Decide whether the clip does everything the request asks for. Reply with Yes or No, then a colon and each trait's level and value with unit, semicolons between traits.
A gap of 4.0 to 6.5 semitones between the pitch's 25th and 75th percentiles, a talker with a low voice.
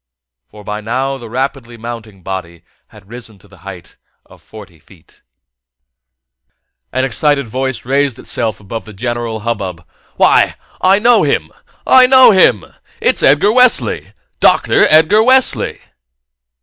Yes: average, 5.3 semitones; low, 120 Hz